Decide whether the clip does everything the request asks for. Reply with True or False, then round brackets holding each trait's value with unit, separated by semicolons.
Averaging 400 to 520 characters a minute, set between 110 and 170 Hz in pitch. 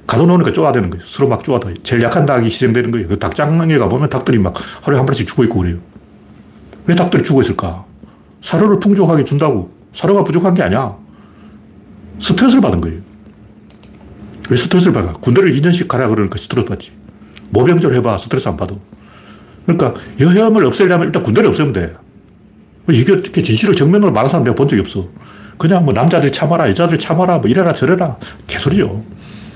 True (420 characters per minute; 135 Hz)